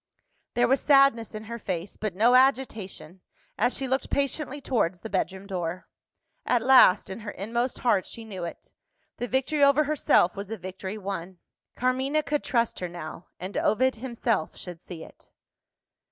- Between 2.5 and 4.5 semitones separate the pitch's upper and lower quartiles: No, wide, 5.6 semitones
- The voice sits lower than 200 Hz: No, high, 225 Hz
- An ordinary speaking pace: Yes, average, 170 wpm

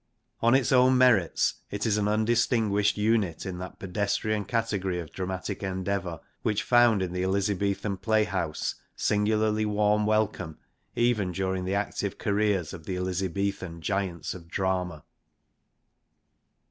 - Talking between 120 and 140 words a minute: Yes, slow, 135 wpm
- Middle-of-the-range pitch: No, low, 100 Hz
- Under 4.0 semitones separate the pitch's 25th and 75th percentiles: Yes, narrow, 2.6 semitones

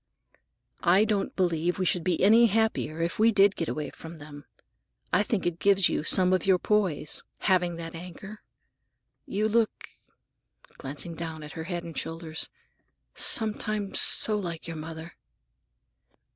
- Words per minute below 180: Yes, average, 150 wpm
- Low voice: No, medium, 175 Hz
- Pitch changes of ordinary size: Yes, average, 3.8 semitones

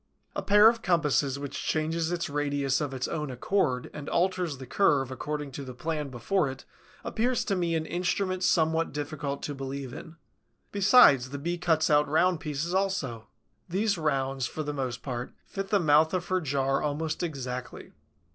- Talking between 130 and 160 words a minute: No, average, 175 wpm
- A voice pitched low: No, medium, 150 Hz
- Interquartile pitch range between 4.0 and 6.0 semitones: Yes, average, 4.4 semitones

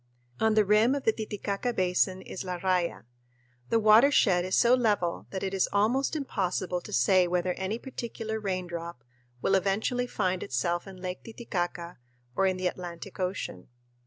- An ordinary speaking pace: Yes, average, 160 wpm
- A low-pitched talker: No, high, 190 Hz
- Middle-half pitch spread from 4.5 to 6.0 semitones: No, average, 3.4 semitones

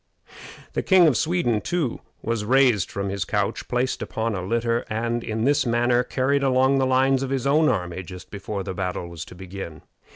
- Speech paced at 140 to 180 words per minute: No, average, 195 wpm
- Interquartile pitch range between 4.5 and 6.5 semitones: Yes, average, 5.1 semitones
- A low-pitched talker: Yes, low, 120 Hz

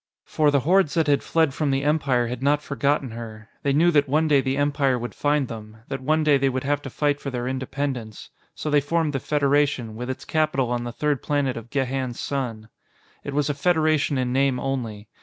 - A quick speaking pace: Yes, fast, 220 wpm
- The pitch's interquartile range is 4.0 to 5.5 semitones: No, average, 2.7 semitones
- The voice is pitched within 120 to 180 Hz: Yes, medium, 140 Hz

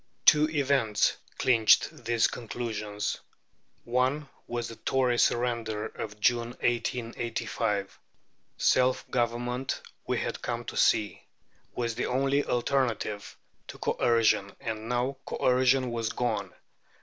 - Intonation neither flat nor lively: No, narrow, 2.2 semitones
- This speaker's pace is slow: Yes, slow, 110 wpm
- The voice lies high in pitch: No, low, 120 Hz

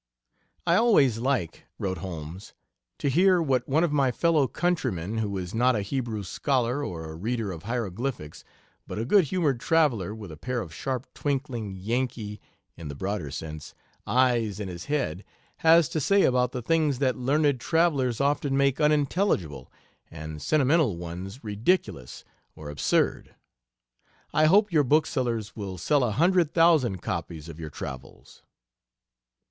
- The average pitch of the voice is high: No, low, 125 Hz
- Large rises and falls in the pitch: Yes, wide, 7.5 semitones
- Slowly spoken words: No, average, 155 wpm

